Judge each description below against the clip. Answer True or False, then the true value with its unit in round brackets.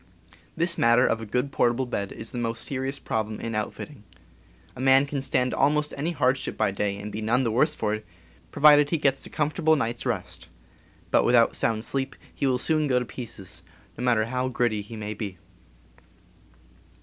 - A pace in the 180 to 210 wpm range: True (195 wpm)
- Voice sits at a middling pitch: False (125 Hz)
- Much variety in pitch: False (4.0 semitones)